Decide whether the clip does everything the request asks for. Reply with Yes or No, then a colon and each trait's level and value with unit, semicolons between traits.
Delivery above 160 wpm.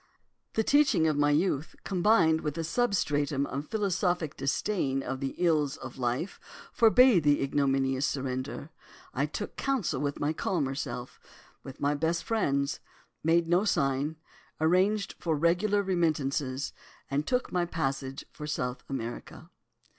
No: average, 140 wpm